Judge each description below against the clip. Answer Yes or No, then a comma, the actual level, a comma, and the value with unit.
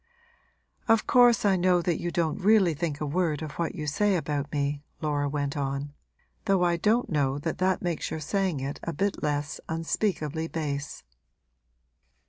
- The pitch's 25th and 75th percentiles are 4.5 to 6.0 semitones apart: No, average, 4.1 semitones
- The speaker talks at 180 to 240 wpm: No, average, 170 wpm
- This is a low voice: No, medium, 160 Hz